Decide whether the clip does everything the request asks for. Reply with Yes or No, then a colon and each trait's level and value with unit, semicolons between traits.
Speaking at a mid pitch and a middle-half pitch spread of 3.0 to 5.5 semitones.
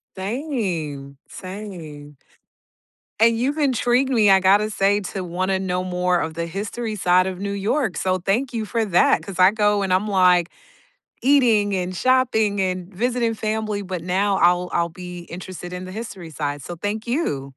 No: high, 195 Hz; average, 3.5 semitones